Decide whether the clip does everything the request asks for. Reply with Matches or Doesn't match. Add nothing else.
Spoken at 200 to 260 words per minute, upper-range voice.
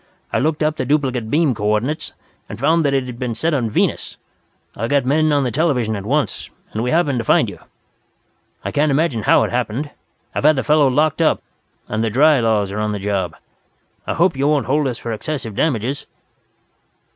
Doesn't match